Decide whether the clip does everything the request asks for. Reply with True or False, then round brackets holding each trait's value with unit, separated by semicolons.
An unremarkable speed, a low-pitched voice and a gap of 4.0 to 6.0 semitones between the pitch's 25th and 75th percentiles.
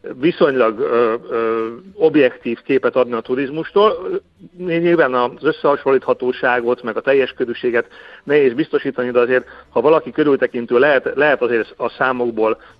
True (125 wpm; 130 Hz; 5.3 semitones)